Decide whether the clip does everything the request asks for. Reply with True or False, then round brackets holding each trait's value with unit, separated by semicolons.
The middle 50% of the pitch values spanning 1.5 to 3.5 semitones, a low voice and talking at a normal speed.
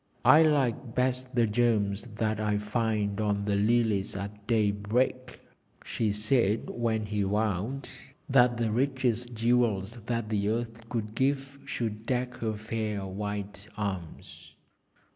False (2.9 semitones; 110 Hz; 130 wpm)